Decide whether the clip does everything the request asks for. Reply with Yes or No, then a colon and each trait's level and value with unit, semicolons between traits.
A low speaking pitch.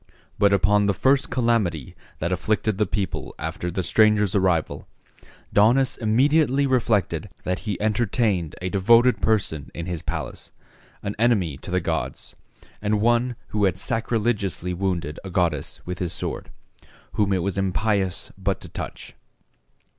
Yes: low, 100 Hz